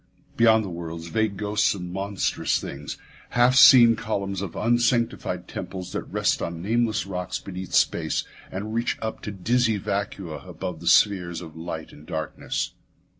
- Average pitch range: Yes, average, 4.3 semitones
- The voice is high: No, low, 100 Hz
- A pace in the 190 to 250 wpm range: No, average, 155 wpm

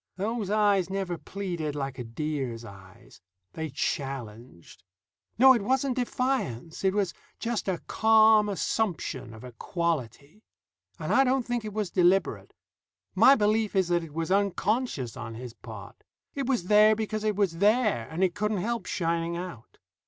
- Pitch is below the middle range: No, high, 190 Hz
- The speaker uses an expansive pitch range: Yes, wide, 6.7 semitones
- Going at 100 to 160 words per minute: Yes, average, 155 wpm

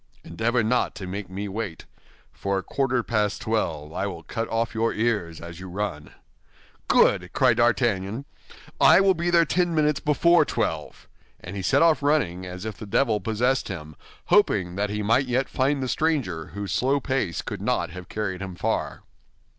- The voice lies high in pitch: No, low, 110 Hz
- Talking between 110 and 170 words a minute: No, average, 180 wpm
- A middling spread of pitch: No, wide, 6.0 semitones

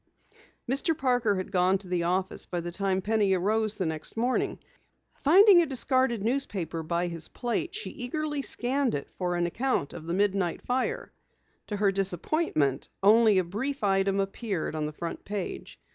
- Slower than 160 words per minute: No, average, 170 wpm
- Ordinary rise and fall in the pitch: No, wide, 5.8 semitones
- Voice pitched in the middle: No, high, 200 Hz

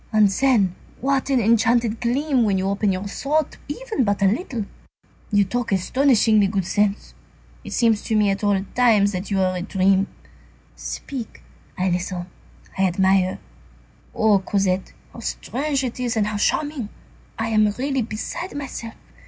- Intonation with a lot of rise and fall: No, average, 4.2 semitones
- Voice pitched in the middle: No, high, 215 Hz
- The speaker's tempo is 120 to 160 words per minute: Yes, average, 155 wpm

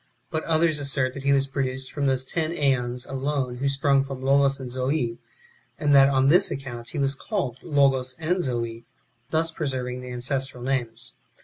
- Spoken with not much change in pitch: Yes, narrow, 1.9 semitones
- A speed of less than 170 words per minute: No, average, 180 wpm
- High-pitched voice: No, low, 135 Hz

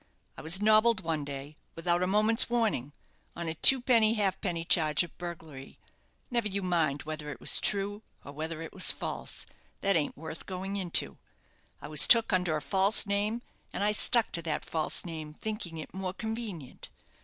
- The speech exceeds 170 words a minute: Yes, average, 180 wpm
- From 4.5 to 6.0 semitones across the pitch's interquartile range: Yes, average, 5.0 semitones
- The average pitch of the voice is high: No, medium, 180 Hz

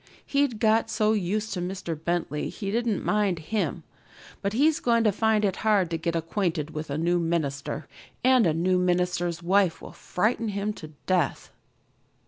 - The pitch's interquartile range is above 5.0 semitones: No, average, 4.3 semitones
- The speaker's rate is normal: Yes, average, 170 wpm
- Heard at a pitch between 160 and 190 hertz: Yes, medium, 185 Hz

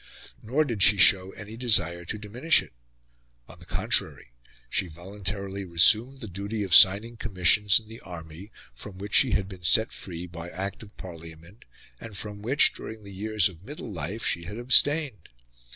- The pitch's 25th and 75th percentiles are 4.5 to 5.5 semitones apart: No, average, 3.7 semitones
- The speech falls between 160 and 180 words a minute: Yes, average, 175 wpm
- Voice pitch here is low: Yes, low, 100 Hz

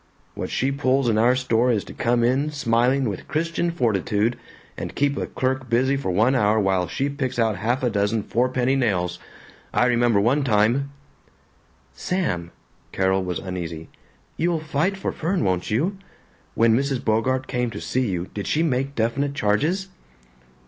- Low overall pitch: Yes, low, 125 Hz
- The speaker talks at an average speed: Yes, average, 170 wpm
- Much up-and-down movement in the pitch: No, average, 4.6 semitones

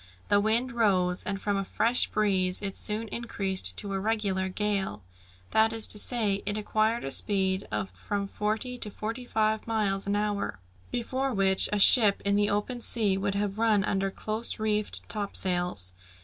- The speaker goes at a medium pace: Yes, average, 175 wpm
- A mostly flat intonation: Yes, narrow, 2.0 semitones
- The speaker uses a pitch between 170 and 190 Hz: No, high, 205 Hz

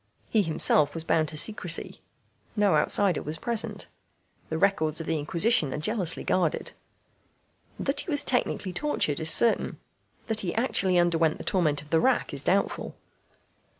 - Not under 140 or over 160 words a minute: Yes, average, 155 wpm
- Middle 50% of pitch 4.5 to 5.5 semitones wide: Yes, average, 5.1 semitones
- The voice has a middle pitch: Yes, medium, 175 Hz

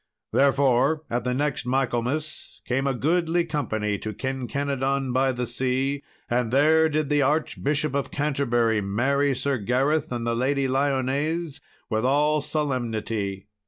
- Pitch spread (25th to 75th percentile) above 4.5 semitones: No, average, 2.9 semitones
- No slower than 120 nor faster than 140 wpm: Yes, slow, 135 wpm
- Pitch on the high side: No, low, 135 Hz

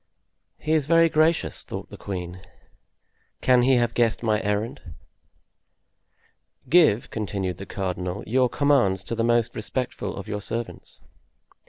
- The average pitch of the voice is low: Yes, low, 115 Hz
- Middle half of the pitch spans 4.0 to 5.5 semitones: Yes, average, 4.6 semitones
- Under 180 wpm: Yes, slow, 135 wpm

